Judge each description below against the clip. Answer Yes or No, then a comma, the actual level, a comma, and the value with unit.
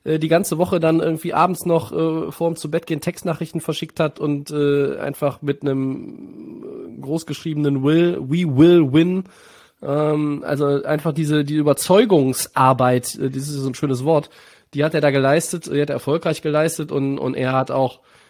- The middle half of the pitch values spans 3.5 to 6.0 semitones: No, average, 2.8 semitones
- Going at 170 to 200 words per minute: Yes, average, 175 wpm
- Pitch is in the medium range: Yes, medium, 155 Hz